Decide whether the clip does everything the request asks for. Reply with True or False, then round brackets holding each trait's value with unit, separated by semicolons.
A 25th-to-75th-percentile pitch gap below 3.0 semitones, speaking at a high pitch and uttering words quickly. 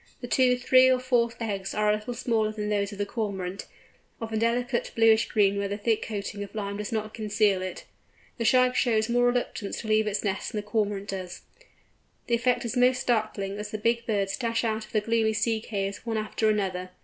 True (2.4 semitones; 215 Hz; 220 wpm)